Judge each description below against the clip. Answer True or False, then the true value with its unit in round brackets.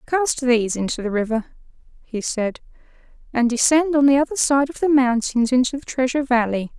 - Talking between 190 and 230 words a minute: False (175 wpm)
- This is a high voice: True (255 Hz)